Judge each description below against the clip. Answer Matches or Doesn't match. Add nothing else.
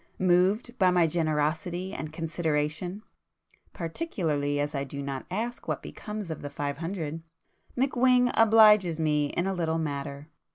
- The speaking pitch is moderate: Matches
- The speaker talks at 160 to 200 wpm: Doesn't match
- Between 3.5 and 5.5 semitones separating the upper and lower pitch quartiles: Matches